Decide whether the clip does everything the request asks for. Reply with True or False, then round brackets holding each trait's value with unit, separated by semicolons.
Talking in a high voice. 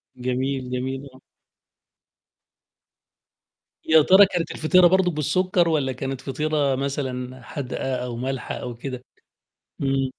False (135 Hz)